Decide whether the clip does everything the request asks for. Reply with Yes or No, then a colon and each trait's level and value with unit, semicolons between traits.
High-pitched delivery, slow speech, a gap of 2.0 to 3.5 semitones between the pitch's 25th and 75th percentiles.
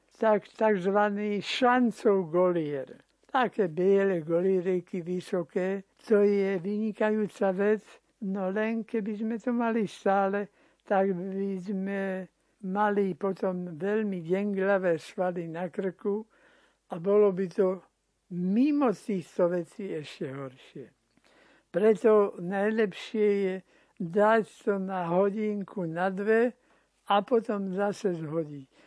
Yes: high, 195 Hz; slow, 105 wpm; narrow, 2.4 semitones